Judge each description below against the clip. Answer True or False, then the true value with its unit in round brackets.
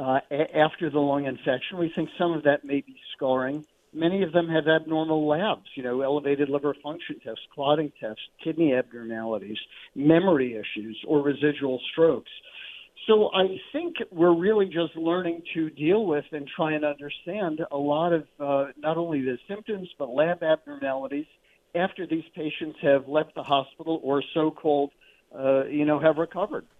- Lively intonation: False (3.1 semitones)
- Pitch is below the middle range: False (155 Hz)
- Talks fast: False (170 wpm)